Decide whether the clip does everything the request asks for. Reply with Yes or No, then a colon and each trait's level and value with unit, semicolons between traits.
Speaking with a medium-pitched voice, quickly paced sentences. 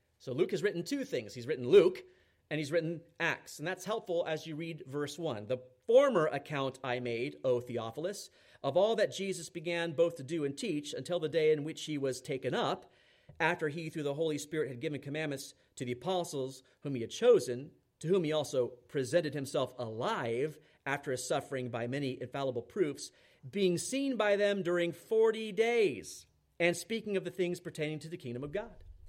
No: medium, 155 Hz; average, 195 wpm